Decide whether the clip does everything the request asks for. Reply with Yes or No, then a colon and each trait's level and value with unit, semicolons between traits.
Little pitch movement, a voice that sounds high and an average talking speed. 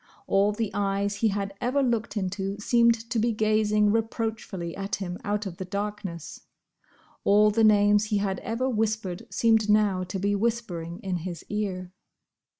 Yes: narrow, 2.2 semitones; high, 205 Hz; average, 160 wpm